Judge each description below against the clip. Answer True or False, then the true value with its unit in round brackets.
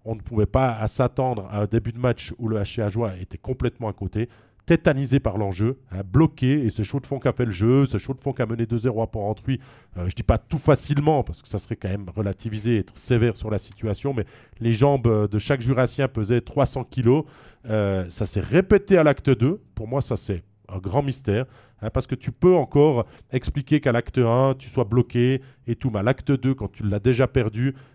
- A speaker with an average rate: False (230 wpm)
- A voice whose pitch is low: True (120 Hz)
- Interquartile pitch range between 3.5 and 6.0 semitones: True (3.8 semitones)